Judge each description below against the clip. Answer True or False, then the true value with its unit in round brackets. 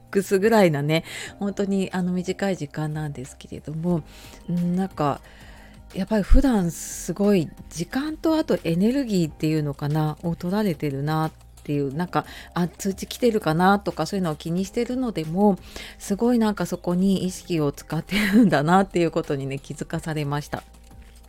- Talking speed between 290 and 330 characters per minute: False (350 characters per minute)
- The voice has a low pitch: False (175 Hz)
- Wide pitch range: False (4.4 semitones)